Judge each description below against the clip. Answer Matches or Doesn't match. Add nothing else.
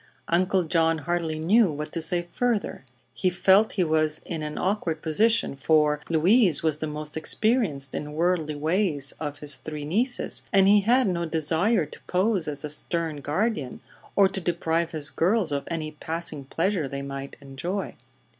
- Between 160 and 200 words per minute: Matches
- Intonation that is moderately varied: Matches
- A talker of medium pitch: Matches